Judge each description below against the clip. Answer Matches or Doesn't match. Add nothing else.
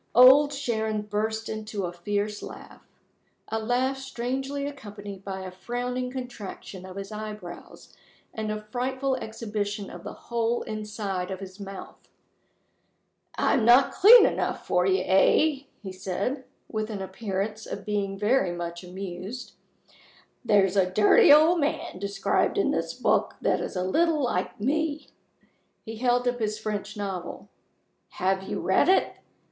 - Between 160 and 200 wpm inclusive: Doesn't match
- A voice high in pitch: Matches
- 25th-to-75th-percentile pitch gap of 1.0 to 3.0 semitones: Doesn't match